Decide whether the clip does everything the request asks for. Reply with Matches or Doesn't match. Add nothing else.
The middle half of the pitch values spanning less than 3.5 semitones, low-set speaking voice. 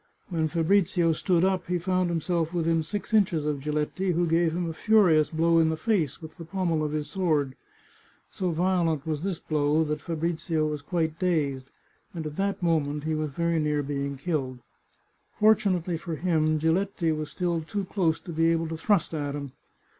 Doesn't match